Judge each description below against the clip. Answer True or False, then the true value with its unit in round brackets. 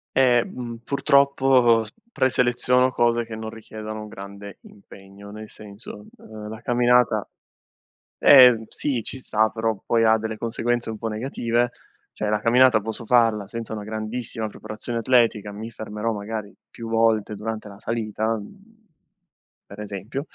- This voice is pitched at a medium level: False (110 Hz)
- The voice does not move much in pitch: True (2.2 semitones)